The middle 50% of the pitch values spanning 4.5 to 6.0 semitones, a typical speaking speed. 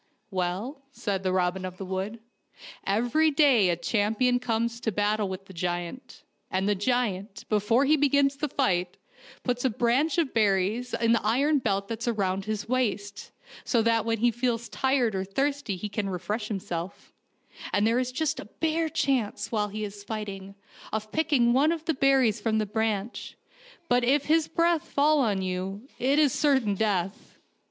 Yes: average, 4.9 semitones; average, 180 wpm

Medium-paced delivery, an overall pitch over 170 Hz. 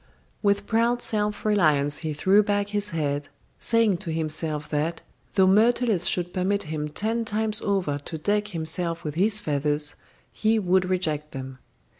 Yes: average, 160 wpm; medium, 185 Hz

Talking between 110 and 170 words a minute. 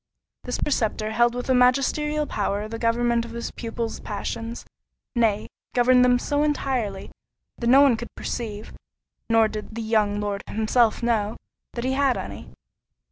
Yes: average, 155 wpm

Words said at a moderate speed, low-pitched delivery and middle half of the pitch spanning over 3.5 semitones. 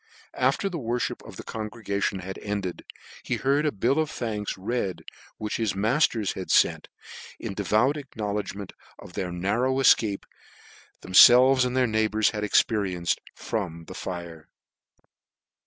Yes: average, 145 wpm; low, 105 Hz; average, 4.3 semitones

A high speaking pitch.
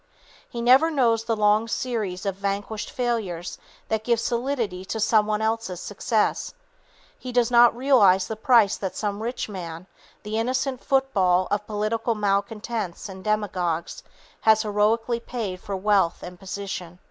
Yes: high, 215 Hz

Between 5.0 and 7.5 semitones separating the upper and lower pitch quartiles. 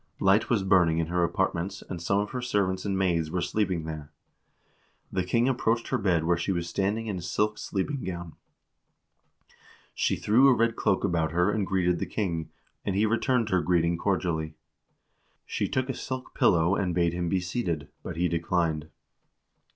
No: average, 3.5 semitones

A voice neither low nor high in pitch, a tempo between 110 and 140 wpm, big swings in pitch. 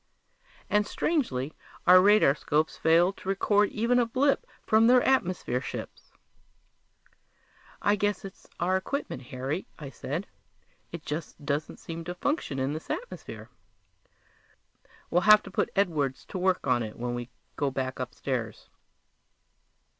Yes: medium, 175 Hz; slow, 135 wpm; wide, 7.2 semitones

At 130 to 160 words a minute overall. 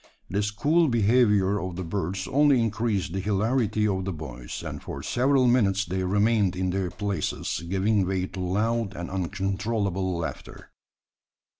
Yes: average, 150 wpm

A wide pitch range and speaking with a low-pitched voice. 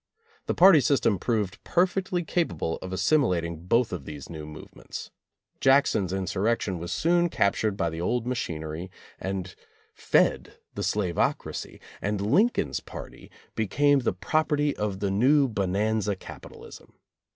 Yes: wide, 7.4 semitones; low, 105 Hz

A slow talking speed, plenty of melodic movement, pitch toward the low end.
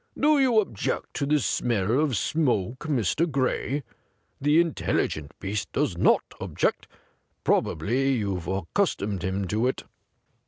Yes: slow, 125 wpm; wide, 7.3 semitones; low, 125 Hz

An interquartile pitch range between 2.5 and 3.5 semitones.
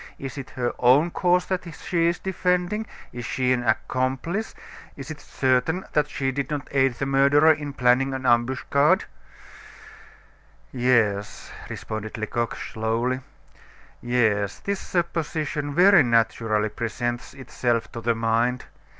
No: average, 4.3 semitones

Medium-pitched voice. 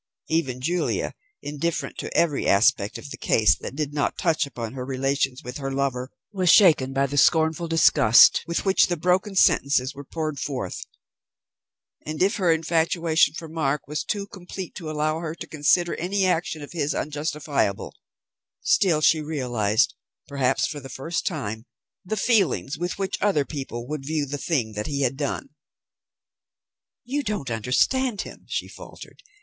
Yes: medium, 150 Hz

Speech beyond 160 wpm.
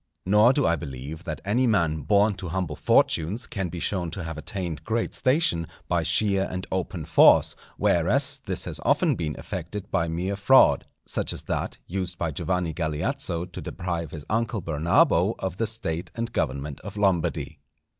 Yes: average, 175 wpm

